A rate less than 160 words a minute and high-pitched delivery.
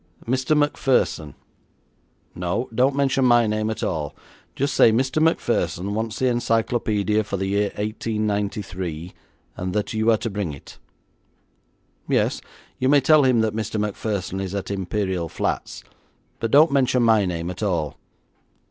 No: average, 150 wpm; low, 110 Hz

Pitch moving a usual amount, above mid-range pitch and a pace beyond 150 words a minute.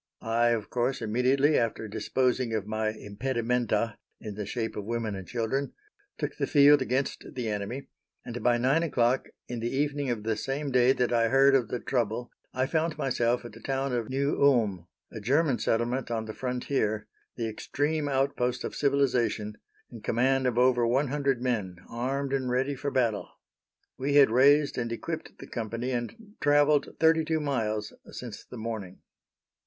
No: average, 3.2 semitones; low, 125 Hz; average, 175 wpm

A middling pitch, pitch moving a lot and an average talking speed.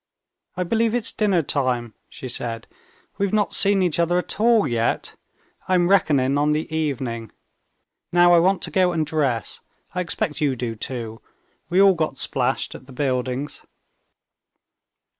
Yes: medium, 155 Hz; wide, 6.1 semitones; average, 160 wpm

